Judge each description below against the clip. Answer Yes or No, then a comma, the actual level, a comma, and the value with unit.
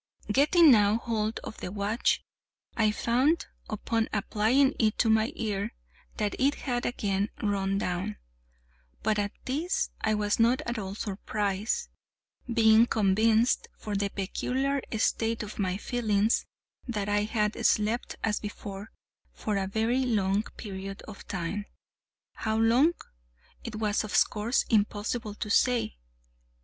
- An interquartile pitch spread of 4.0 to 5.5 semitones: No, narrow, 2.4 semitones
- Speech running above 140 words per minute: No, slow, 135 wpm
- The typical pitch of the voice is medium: No, high, 215 Hz